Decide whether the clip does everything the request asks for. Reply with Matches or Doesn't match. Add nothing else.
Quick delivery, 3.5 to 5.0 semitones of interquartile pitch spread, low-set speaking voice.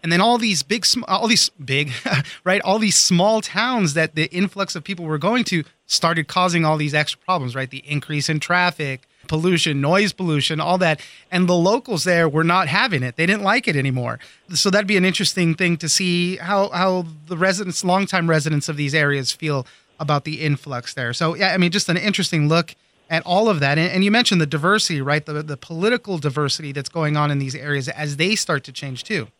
Doesn't match